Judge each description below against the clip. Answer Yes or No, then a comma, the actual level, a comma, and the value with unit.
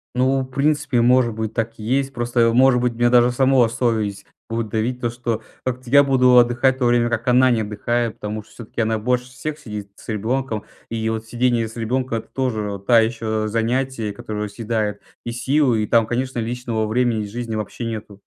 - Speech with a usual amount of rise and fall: No, narrow, 2.3 semitones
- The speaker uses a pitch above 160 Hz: No, low, 120 Hz